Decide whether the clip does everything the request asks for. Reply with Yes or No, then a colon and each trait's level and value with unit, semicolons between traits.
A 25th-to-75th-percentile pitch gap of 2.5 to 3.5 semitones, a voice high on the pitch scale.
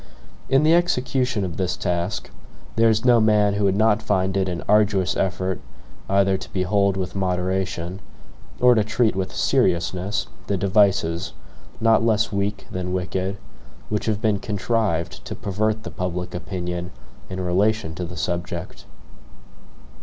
No: average, 3.0 semitones; very low, 95 Hz